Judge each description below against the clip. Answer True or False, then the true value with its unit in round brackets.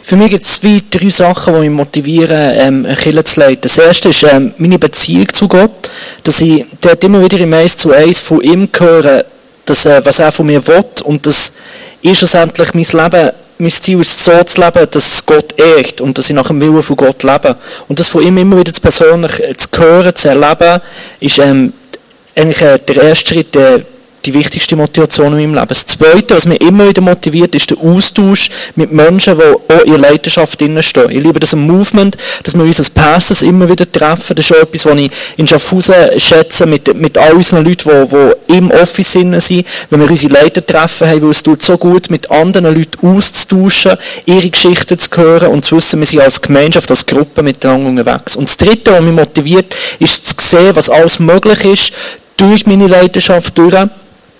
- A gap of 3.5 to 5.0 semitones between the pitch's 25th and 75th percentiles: False (3.1 semitones)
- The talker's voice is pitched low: False (165 Hz)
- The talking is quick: True (210 wpm)